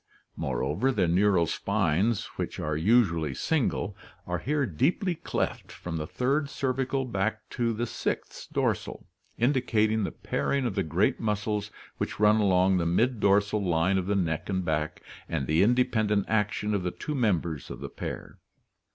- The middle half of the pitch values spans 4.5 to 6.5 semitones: Yes, wide, 5.4 semitones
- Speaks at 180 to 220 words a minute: No, average, 160 wpm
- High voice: No, low, 105 Hz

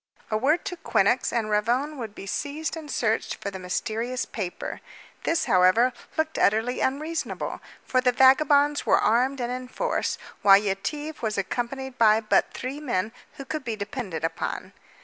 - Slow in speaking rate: No, average, 165 wpm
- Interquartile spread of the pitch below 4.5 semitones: No, average, 5.0 semitones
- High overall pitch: Yes, very high, 250 Hz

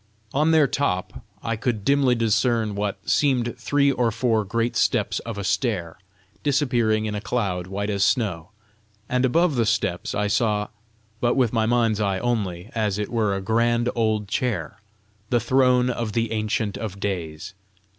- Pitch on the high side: No, low, 115 Hz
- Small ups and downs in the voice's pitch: No, average, 3.2 semitones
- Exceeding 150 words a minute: Yes, average, 165 wpm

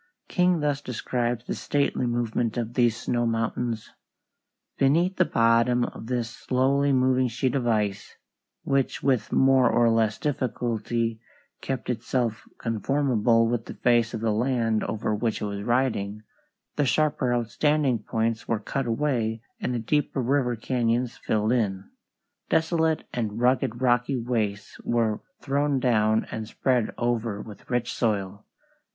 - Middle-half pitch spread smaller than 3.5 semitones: Yes, narrow, 2.6 semitones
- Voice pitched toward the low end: Yes, low, 120 Hz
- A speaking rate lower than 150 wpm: Yes, average, 140 wpm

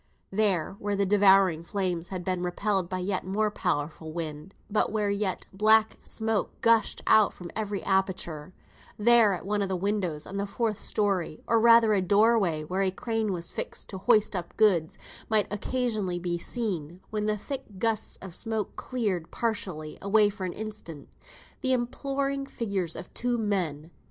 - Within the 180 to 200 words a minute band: No, average, 170 wpm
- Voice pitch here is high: Yes, high, 200 Hz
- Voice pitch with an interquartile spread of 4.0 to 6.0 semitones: No, average, 3.4 semitones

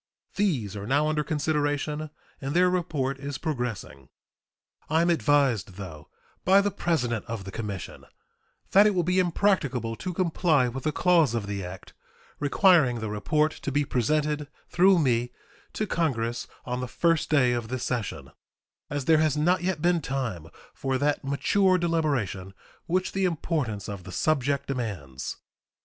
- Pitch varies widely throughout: Yes, wide, 5.9 semitones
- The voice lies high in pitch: No, medium, 145 Hz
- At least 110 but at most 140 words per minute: No, average, 160 wpm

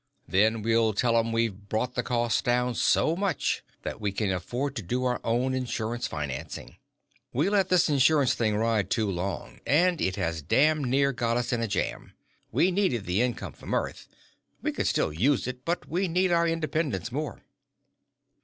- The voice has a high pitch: No, low, 120 Hz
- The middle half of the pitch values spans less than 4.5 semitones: No, average, 5.1 semitones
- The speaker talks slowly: No, average, 180 wpm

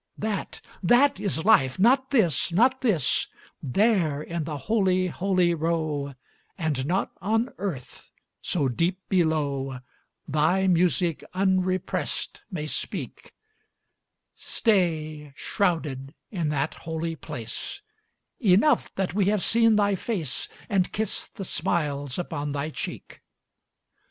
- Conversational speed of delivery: No, slow, 115 wpm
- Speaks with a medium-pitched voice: Yes, medium, 175 Hz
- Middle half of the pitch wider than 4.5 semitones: Yes, average, 5.0 semitones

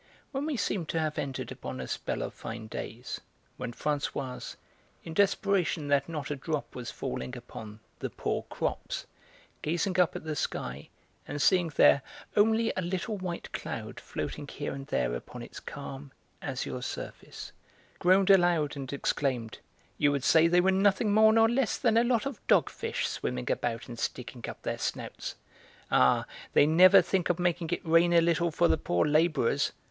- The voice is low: No, medium, 160 Hz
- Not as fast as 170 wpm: No, average, 175 wpm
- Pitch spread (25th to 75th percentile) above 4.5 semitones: Yes, wide, 5.5 semitones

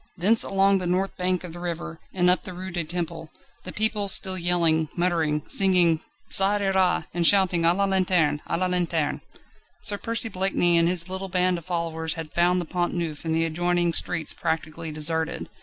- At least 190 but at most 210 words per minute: Yes, average, 195 wpm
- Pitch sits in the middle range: Yes, medium, 175 Hz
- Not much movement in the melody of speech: Yes, narrow, 2.2 semitones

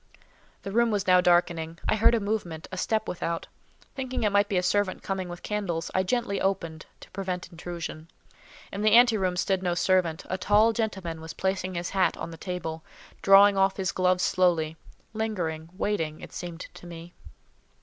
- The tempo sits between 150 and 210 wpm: Yes, average, 180 wpm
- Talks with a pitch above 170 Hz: Yes, medium, 185 Hz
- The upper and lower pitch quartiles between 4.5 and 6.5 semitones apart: No, average, 3.0 semitones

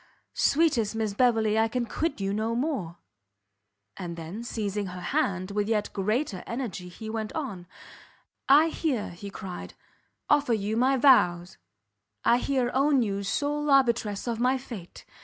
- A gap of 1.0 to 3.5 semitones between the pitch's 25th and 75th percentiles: No, average, 4.8 semitones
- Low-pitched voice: No, high, 225 Hz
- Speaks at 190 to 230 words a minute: No, average, 150 wpm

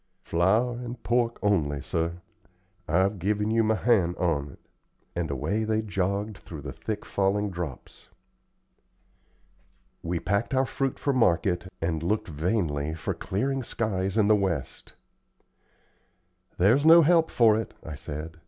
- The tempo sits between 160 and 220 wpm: No, average, 140 wpm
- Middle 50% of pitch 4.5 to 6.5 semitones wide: Yes, average, 4.9 semitones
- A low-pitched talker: Yes, low, 100 Hz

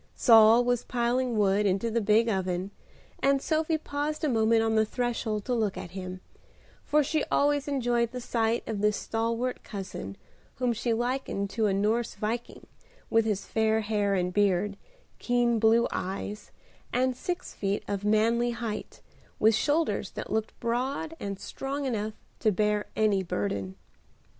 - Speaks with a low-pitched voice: No, high, 225 Hz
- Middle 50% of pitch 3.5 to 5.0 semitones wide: No, average, 2.9 semitones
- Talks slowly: No, average, 155 wpm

